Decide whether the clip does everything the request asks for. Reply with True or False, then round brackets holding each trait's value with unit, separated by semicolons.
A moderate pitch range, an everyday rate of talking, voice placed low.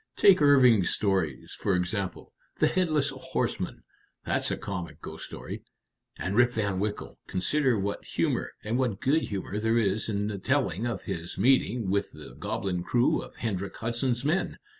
True (4.5 semitones; 160 wpm; 105 Hz)